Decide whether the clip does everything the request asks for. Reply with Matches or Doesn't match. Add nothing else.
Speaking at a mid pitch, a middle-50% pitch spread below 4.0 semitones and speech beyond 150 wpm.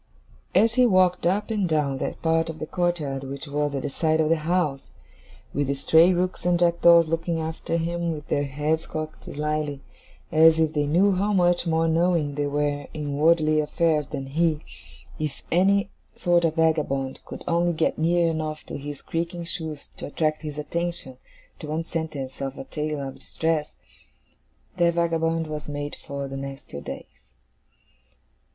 Matches